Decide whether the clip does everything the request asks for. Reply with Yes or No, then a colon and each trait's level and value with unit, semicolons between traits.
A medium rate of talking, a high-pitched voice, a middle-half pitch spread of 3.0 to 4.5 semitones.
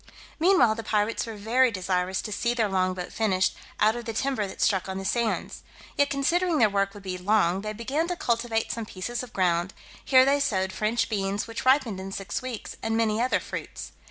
No: fast, 215 wpm; high, 220 Hz; average, 3.9 semitones